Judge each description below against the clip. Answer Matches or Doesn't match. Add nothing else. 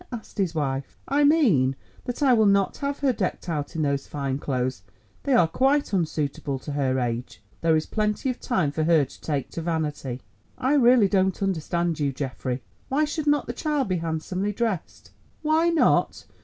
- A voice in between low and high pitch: Matches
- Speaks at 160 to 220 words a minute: Matches